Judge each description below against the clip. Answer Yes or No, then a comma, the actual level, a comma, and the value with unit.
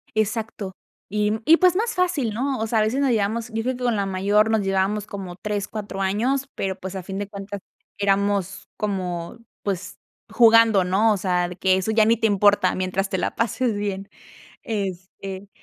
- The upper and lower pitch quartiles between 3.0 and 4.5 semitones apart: No, narrow, 2.6 semitones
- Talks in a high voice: Yes, high, 205 Hz